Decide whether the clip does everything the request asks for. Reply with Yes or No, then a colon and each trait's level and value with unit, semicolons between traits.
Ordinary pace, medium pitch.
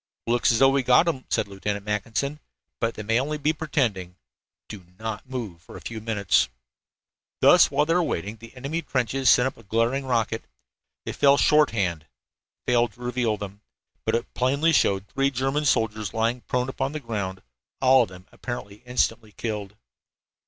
No: average, 175 wpm; low, 115 Hz